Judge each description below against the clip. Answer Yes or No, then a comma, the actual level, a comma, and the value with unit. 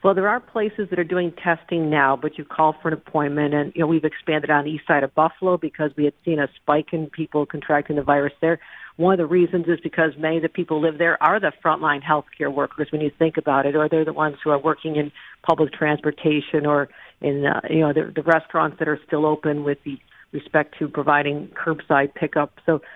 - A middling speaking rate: No, fast, 240 wpm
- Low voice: No, medium, 155 Hz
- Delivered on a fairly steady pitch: Yes, narrow, 1.8 semitones